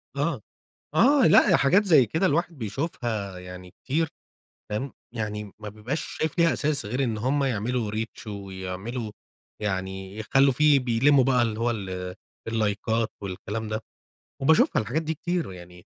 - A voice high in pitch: No, low, 115 Hz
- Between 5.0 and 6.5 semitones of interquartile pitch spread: Yes, wide, 5.6 semitones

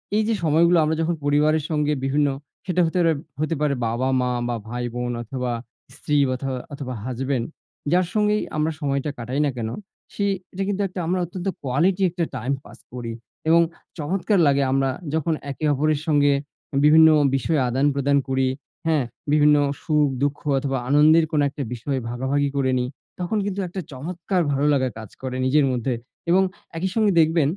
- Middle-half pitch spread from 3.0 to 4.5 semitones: Yes, average, 3.8 semitones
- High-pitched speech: No, medium, 145 Hz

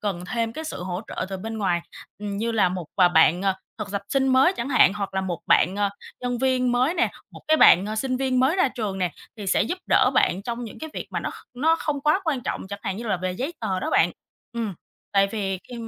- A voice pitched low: No, high, 215 Hz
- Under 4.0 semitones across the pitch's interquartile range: No, average, 5.2 semitones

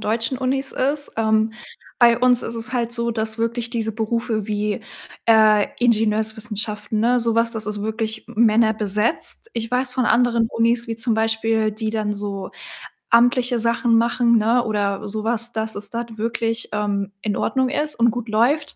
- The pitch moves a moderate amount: No, narrow, 1.6 semitones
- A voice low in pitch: No, high, 225 Hz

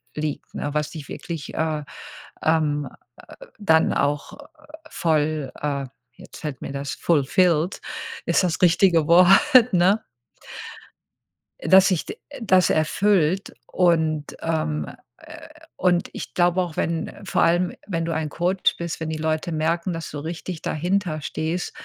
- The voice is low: No, medium, 165 Hz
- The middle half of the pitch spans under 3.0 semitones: Yes, narrow, 2.6 semitones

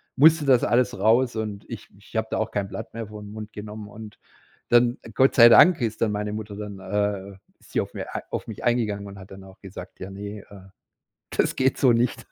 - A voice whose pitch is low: Yes, low, 105 Hz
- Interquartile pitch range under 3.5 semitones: Yes, narrow, 2.6 semitones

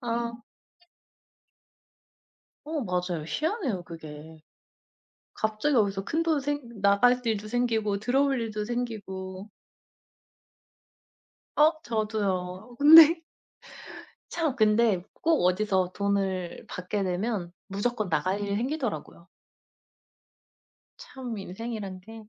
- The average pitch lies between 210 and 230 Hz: Yes, high, 215 Hz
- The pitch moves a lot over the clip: No, average, 4.7 semitones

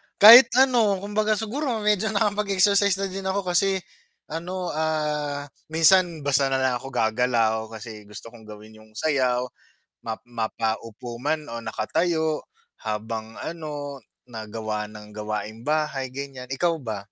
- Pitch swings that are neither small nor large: No, wide, 8.5 semitones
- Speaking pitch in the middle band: Yes, medium, 145 Hz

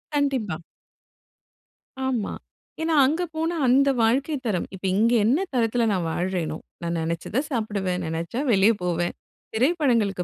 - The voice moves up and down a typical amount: No, wide, 6.7 semitones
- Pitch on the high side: Yes, high, 220 Hz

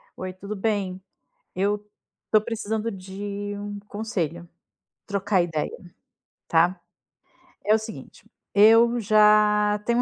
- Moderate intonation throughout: No, narrow, 2.1 semitones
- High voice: Yes, high, 205 Hz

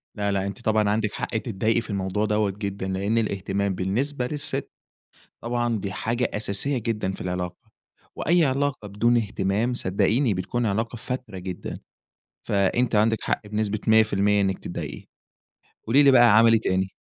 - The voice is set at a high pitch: No, low, 105 Hz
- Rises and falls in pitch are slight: No, average, 3.1 semitones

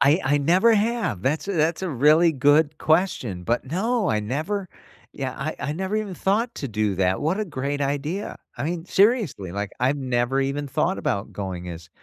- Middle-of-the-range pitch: Yes, medium, 145 Hz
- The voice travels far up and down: Yes, wide, 6.8 semitones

